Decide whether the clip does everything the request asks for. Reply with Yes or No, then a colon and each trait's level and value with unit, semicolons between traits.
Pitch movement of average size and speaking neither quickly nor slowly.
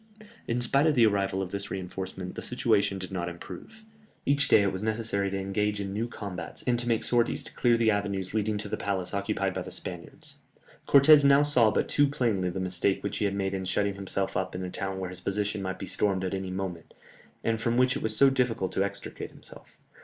No: average, 3.4 semitones; fast, 230 wpm